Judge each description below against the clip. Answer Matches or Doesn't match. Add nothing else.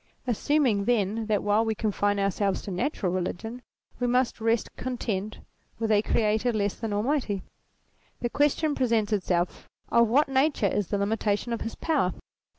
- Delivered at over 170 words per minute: Doesn't match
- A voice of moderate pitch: Doesn't match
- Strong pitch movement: Doesn't match